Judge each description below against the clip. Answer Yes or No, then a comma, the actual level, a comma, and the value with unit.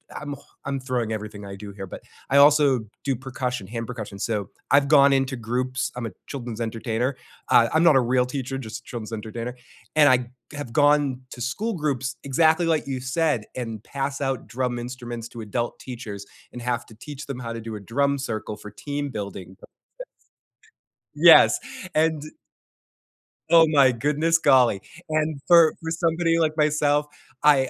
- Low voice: Yes, low, 130 Hz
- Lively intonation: No, average, 3.9 semitones